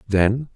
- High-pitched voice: No, low, 110 Hz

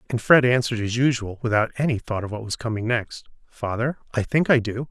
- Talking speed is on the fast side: Yes, fast, 220 wpm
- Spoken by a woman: No, male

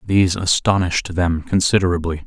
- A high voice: No, very low, 90 Hz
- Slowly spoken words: Yes, slow, 105 wpm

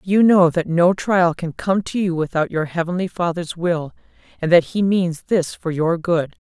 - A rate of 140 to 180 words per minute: No, fast, 205 wpm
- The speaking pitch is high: No, medium, 175 Hz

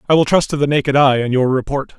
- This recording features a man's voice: Yes, male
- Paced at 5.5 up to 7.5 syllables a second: Yes, 6.6 syllables/s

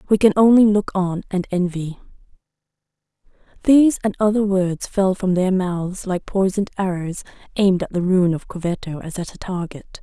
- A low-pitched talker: No, high, 190 Hz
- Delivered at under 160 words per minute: No, average, 170 wpm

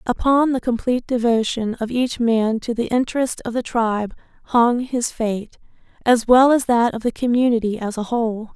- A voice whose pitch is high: Yes, high, 235 Hz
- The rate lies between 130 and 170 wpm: No, average, 180 wpm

